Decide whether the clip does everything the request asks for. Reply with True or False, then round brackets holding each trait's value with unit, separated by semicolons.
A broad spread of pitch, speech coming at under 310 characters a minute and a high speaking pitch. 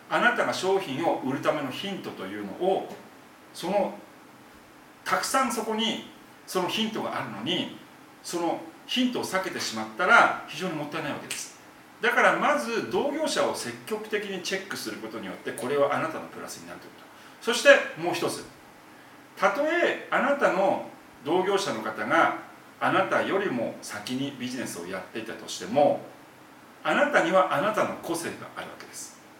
False (8.8 semitones; 345 characters per minute; 195 Hz)